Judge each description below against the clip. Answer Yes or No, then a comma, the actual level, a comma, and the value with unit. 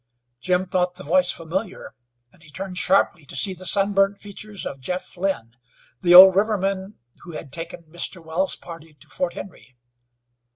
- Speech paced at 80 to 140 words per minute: No, average, 170 wpm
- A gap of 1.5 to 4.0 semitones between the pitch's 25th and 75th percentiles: Yes, average, 2.8 semitones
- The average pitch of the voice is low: No, medium, 180 Hz